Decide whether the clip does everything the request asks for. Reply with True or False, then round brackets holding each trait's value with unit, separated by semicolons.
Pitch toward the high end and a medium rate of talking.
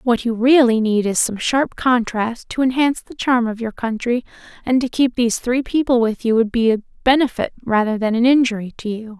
False (235 Hz; 215 wpm)